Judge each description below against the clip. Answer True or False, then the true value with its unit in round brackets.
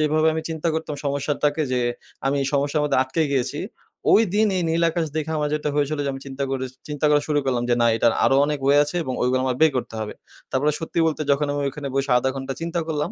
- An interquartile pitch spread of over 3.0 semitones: False (2.6 semitones)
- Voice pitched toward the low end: False (145 Hz)